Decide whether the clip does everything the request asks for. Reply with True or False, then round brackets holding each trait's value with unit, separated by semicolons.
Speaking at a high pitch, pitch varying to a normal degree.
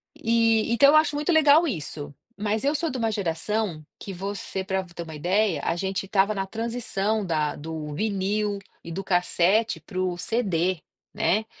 True (200 Hz; 4.1 semitones)